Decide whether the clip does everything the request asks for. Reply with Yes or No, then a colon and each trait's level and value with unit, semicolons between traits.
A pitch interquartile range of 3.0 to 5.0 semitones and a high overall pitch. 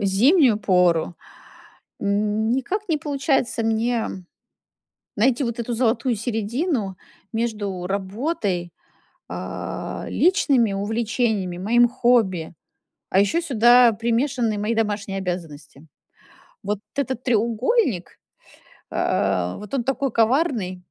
Yes: average, 4.1 semitones; high, 225 Hz